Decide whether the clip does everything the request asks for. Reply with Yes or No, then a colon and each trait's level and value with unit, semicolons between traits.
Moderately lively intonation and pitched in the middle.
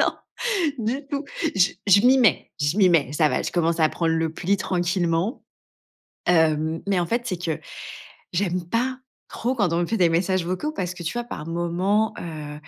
Yes: average, 3.7 semitones; medium, 175 Hz